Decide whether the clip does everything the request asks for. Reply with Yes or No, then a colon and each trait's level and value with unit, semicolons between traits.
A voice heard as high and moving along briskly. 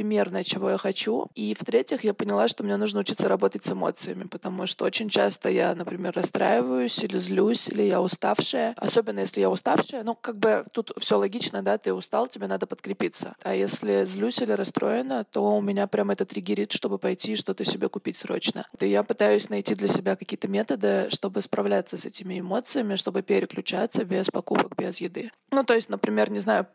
Yes: high, 195 Hz; fast, 195 wpm